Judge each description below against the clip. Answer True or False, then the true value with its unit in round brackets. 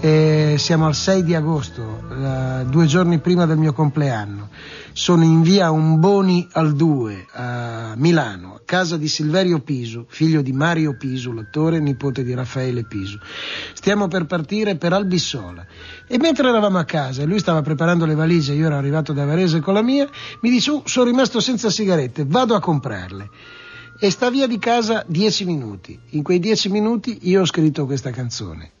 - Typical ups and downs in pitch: False (6.0 semitones)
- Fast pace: True (180 wpm)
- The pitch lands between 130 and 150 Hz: False (160 Hz)